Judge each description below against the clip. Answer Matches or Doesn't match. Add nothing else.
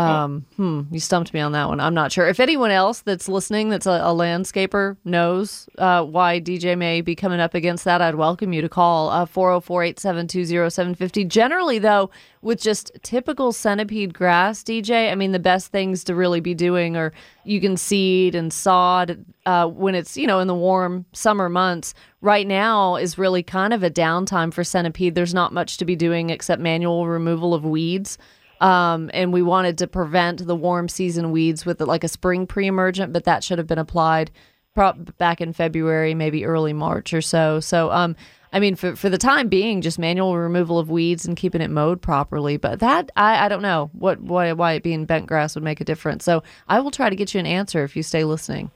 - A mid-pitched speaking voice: Matches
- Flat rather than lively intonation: Matches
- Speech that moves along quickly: Matches